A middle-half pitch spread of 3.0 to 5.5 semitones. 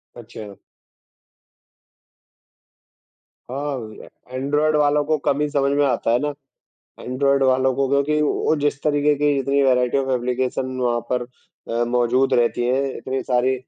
No: narrow, 2.5 semitones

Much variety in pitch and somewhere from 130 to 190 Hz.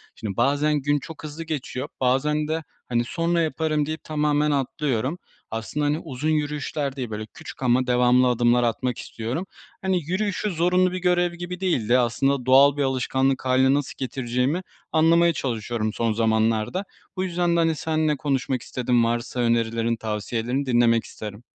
No: average, 4.7 semitones; low, 135 Hz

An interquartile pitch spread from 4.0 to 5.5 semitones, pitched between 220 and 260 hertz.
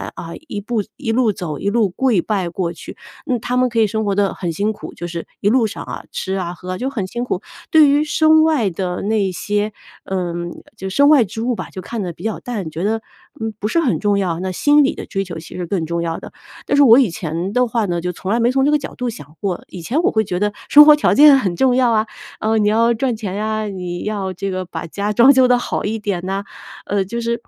No: average, 4.8 semitones; high, 210 Hz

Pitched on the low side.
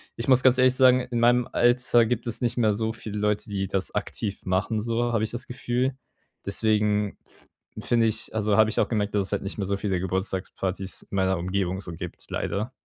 Yes: low, 105 Hz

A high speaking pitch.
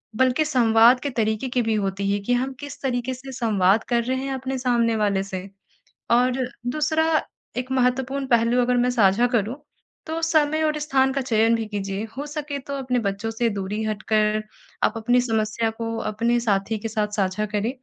Yes: high, 240 Hz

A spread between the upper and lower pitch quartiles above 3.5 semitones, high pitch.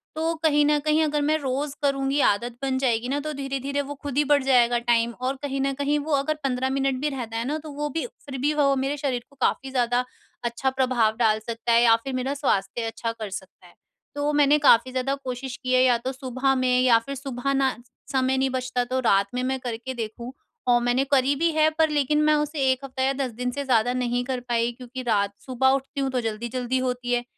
No: narrow, 2.5 semitones; very high, 260 Hz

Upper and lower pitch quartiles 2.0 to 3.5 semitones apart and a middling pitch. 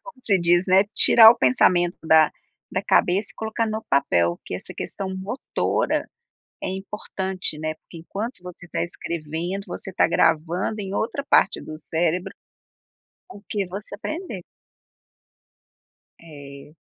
No: average, 4.0 semitones; medium, 180 Hz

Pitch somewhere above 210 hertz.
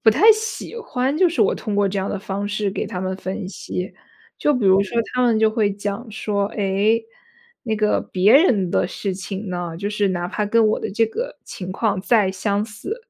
No: high, 205 Hz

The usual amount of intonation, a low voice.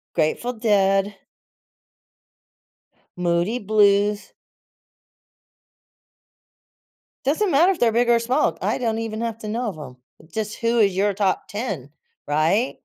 No: average, 3.3 semitones; high, 215 Hz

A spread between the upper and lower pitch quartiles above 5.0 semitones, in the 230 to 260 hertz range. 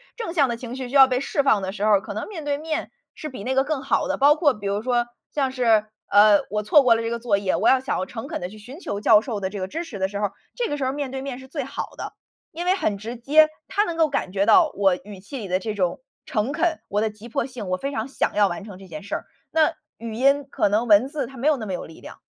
Yes: wide, 5.6 semitones; high, 240 Hz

